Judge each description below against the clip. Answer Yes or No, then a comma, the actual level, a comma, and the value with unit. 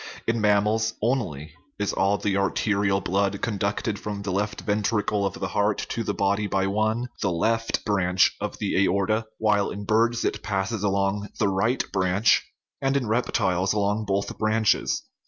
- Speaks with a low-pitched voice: Yes, low, 105 Hz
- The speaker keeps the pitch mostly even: Yes, narrow, 1.9 semitones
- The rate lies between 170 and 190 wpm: Yes, average, 180 wpm